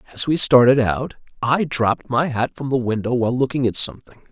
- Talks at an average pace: No, fast, 210 wpm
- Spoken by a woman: No, male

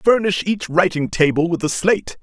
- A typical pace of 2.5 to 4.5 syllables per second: No, 5.2 syllables/s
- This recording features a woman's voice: No, male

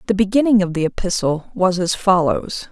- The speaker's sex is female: Yes, female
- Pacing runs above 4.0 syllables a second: Yes, 5.3 syllables/s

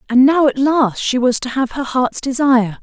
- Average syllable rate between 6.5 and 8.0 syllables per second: No, 4.9 syllables/s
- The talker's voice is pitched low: No, very high, 260 Hz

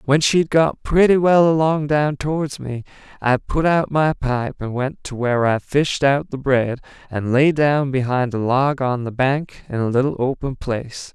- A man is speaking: Yes, male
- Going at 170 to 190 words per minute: No, average, 200 wpm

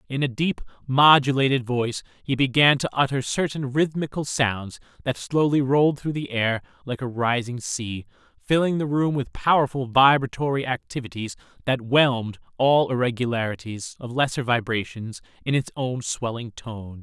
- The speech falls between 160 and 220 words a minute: No, average, 145 wpm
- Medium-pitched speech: No, low, 125 Hz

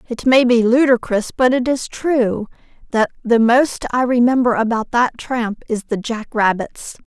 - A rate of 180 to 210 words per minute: No, average, 170 wpm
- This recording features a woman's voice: Yes, female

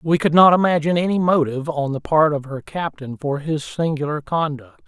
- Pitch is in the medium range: Yes, medium, 155 Hz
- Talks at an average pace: Yes, average, 195 wpm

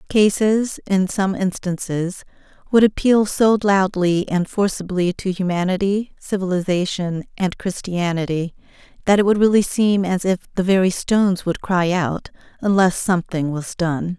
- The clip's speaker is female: Yes, female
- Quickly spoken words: No, slow, 135 wpm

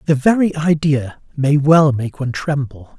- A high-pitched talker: No, medium, 145 Hz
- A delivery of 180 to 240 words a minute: No, average, 160 wpm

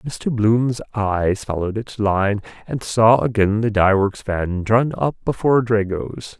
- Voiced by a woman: No, male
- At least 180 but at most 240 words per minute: No, average, 150 wpm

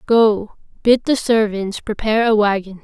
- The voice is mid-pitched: No, high, 215 Hz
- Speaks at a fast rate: No, average, 150 wpm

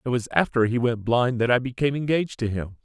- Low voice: Yes, low, 125 Hz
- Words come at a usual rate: No, fast, 255 wpm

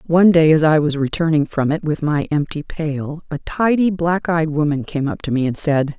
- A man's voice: No, female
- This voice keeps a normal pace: No, fast, 230 wpm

